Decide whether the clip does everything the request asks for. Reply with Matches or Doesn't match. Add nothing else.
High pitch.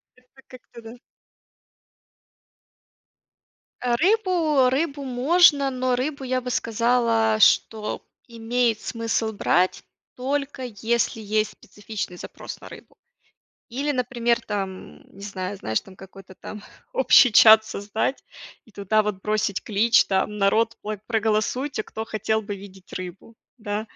Matches